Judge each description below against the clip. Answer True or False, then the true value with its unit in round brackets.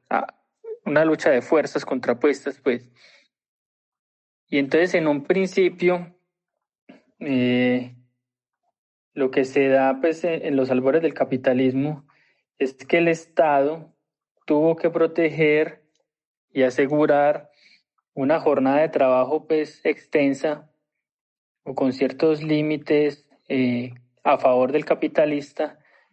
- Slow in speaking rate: True (105 wpm)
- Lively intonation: False (2.9 semitones)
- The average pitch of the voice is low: False (150 Hz)